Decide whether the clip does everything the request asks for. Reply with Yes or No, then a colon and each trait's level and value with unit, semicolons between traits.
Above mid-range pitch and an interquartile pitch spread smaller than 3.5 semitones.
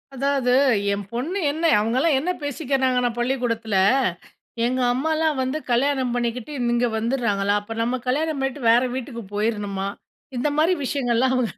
Yes: very high, 255 Hz; average, 3.1 semitones